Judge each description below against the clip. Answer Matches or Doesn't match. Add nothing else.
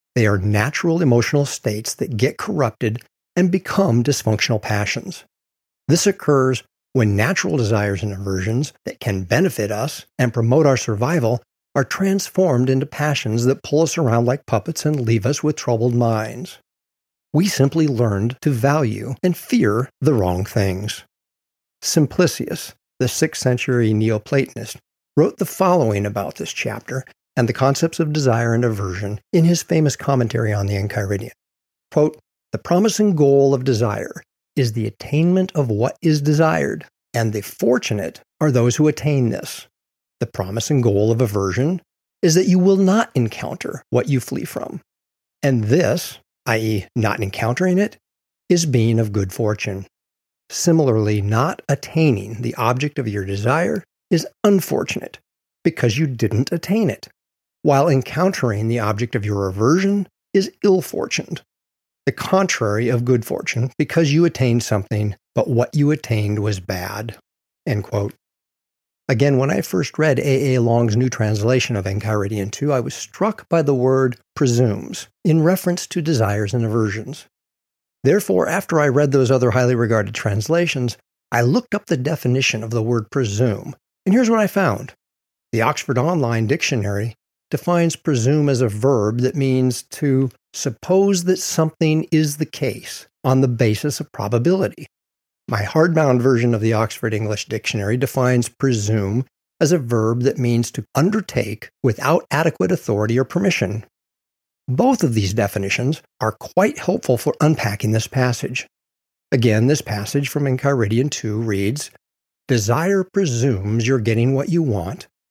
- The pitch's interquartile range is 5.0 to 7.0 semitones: Matches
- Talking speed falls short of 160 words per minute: Matches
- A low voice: Matches